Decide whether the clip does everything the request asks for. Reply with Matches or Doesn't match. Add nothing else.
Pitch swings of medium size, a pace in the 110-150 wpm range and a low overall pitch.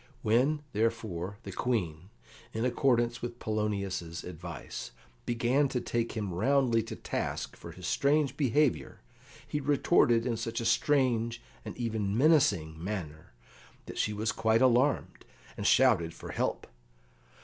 Matches